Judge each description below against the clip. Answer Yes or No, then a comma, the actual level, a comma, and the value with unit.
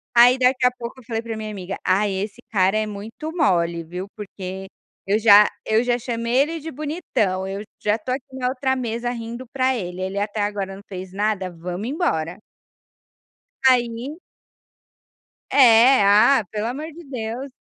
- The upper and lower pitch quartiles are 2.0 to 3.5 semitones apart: No, average, 4.4 semitones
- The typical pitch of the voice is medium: No, high, 225 Hz